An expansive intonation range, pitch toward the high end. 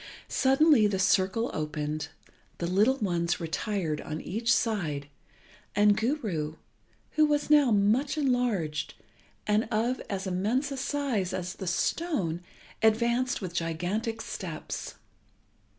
Yes: wide, 6.2 semitones; high, 210 Hz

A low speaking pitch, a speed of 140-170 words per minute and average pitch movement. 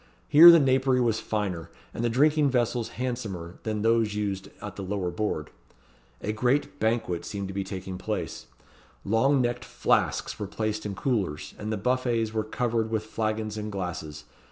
Yes: low, 110 Hz; average, 160 wpm; average, 3.7 semitones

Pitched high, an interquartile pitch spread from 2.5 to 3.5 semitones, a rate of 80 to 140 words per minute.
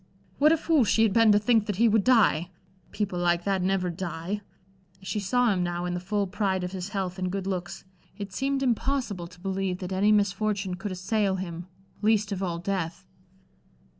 No: high, 195 Hz; average, 2.8 semitones; average, 200 wpm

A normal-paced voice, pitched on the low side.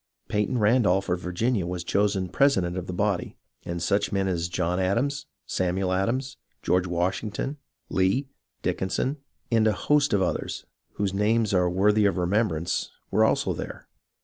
Yes: average, 150 wpm; very low, 95 Hz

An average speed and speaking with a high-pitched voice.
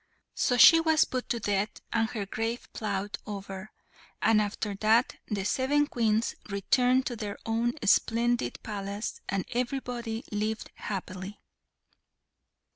No: slow, 125 wpm; high, 220 Hz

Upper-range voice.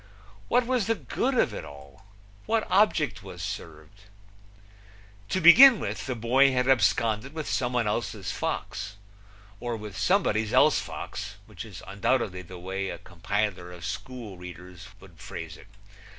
No: low, 105 Hz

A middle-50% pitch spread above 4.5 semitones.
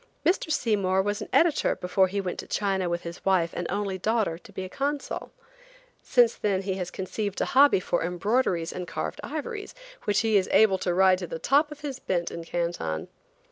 No: average, 4.1 semitones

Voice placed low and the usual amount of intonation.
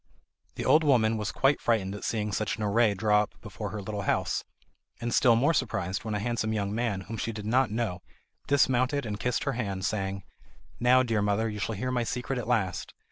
Yes: low, 110 Hz; average, 3.0 semitones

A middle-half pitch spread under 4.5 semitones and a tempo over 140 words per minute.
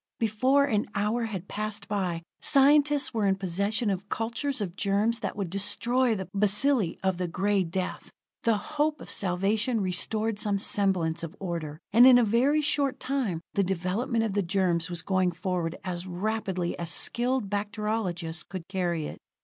Yes: average, 4.0 semitones; average, 165 wpm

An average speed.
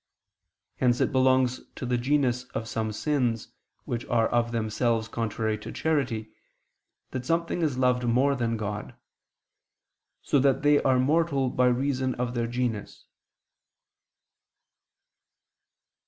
No: slow, 125 wpm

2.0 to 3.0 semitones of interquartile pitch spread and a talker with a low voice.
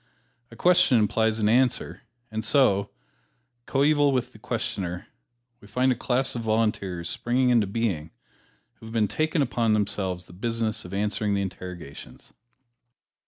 No: average, 3.9 semitones; low, 110 Hz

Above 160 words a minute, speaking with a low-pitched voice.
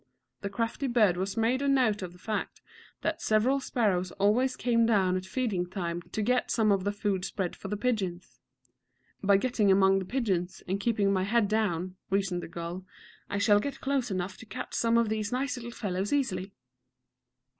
No: average, 190 wpm; high, 205 Hz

